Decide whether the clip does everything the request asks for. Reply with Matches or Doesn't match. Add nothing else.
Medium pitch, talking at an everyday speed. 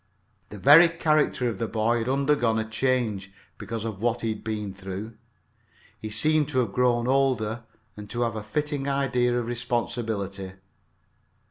Doesn't match